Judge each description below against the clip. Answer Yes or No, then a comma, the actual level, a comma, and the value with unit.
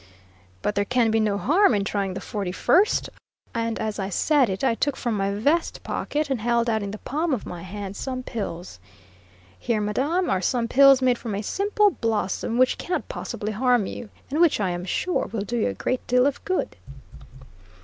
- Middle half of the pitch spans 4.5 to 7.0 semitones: Yes, average, 5.0 semitones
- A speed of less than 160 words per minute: No, fast, 205 wpm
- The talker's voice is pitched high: Yes, high, 230 Hz